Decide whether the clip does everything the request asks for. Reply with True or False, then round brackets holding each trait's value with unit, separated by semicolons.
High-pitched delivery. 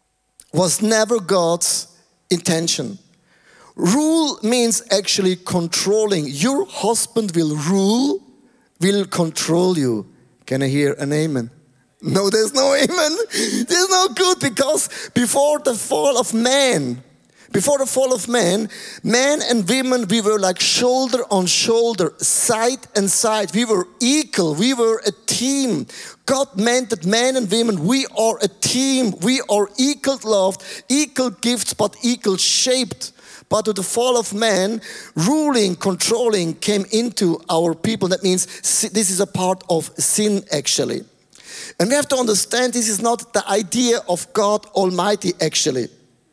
True (220 Hz)